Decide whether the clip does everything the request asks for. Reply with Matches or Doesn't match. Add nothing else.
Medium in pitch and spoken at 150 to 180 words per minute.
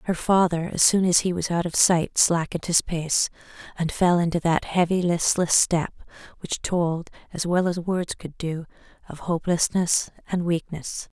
Matches